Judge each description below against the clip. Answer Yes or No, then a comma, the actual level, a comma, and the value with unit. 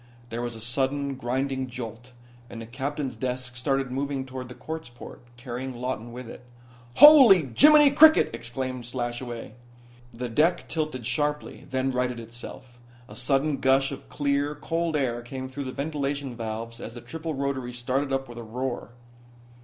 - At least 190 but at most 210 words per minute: No, average, 160 wpm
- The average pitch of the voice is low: Yes, low, 130 Hz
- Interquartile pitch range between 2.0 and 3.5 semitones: Yes, average, 2.7 semitones